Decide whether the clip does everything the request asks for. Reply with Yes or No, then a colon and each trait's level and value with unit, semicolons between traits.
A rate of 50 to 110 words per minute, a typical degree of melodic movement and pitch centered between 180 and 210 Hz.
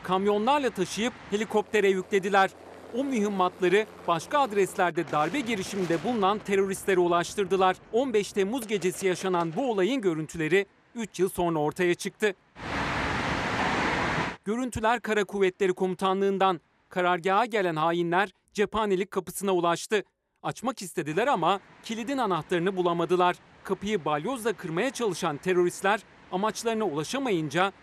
Yes: average, 105 wpm; average, 3.0 semitones; high, 190 Hz